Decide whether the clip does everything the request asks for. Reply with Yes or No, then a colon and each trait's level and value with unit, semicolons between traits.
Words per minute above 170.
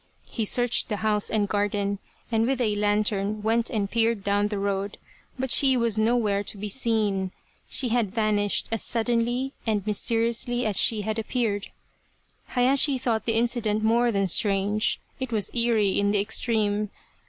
No: average, 165 wpm